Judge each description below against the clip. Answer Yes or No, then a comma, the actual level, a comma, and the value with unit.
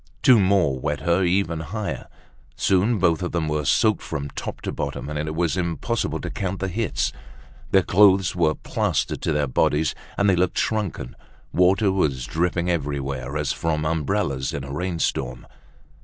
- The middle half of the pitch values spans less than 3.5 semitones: No, average, 4.4 semitones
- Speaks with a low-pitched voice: Yes, very low, 85 Hz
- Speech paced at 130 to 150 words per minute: No, average, 170 wpm